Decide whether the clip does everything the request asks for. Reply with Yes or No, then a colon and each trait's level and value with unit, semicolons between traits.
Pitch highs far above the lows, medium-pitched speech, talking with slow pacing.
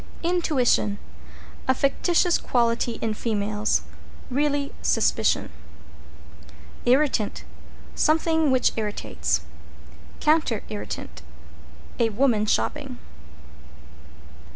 No: wide, 5.7 semitones; very high, 250 Hz; slow, 70 wpm